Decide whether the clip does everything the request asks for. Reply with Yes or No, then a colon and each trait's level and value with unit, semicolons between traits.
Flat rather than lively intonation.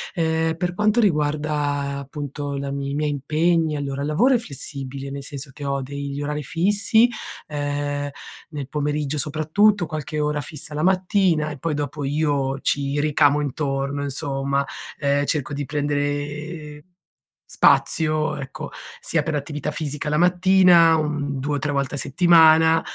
Yes: narrow, 2.1 semitones